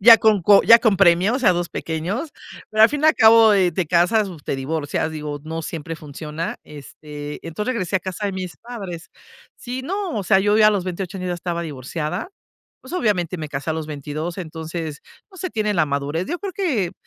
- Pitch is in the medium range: Yes, medium, 180 Hz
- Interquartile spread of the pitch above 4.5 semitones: Yes, wide, 5.4 semitones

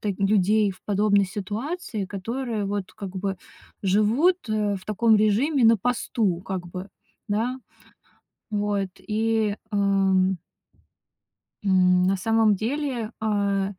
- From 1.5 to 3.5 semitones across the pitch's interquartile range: Yes, narrow, 2.4 semitones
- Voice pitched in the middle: No, high, 205 Hz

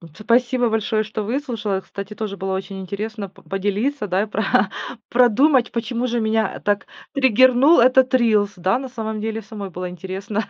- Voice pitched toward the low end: No, high, 220 Hz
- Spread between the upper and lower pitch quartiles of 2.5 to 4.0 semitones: Yes, average, 3.3 semitones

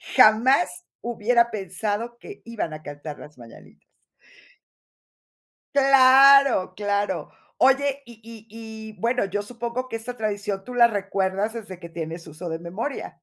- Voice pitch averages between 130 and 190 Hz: No, high, 215 Hz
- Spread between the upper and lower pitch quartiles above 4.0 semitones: Yes, average, 4.5 semitones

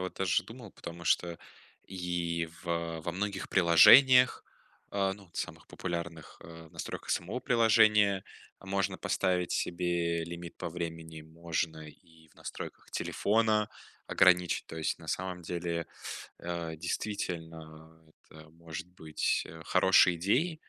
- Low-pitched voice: Yes, very low, 85 Hz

